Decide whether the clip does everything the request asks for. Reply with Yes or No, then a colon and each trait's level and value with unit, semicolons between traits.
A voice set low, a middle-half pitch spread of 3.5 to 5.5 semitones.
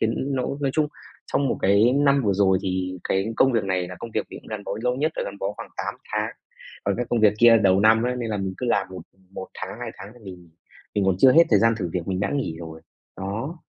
Yes: low, 105 Hz; average, 4.5 semitones